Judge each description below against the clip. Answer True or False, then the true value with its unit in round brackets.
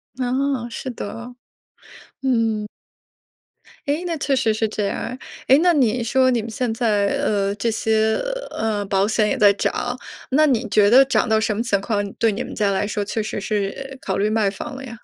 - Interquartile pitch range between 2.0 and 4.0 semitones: True (3.4 semitones)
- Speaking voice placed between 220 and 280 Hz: True (225 Hz)